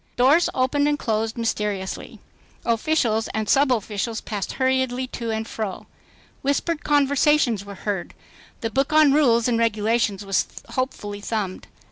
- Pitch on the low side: No, high, 230 Hz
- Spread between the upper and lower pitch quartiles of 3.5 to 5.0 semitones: Yes, average, 4.2 semitones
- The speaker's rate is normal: No, slow, 130 wpm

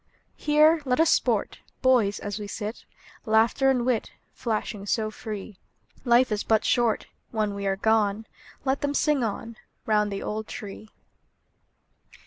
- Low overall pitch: No, high, 220 Hz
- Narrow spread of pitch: No, average, 3.2 semitones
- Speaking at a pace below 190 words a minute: Yes, average, 145 wpm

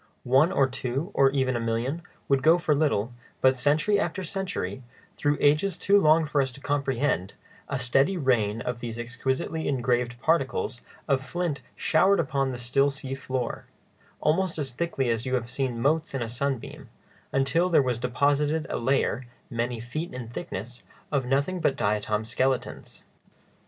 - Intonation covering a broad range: No, average, 3.9 semitones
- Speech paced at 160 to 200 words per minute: Yes, average, 165 wpm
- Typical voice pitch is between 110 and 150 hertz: Yes, low, 135 Hz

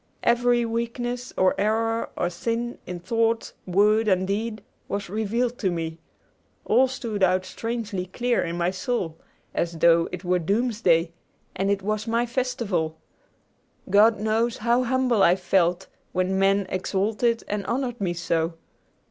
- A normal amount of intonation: Yes, average, 4.2 semitones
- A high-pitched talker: Yes, high, 210 Hz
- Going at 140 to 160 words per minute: Yes, average, 145 wpm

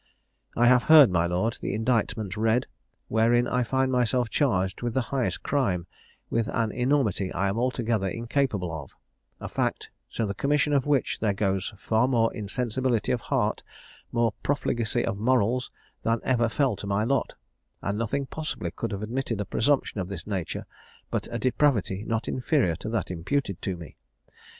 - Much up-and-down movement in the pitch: No, average, 4.2 semitones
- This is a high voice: No, low, 115 Hz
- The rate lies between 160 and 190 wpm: Yes, average, 170 wpm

